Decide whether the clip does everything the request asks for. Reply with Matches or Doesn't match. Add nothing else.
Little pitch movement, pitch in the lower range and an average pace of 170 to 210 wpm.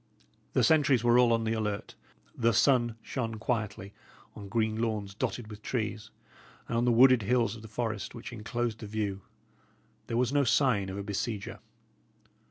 Matches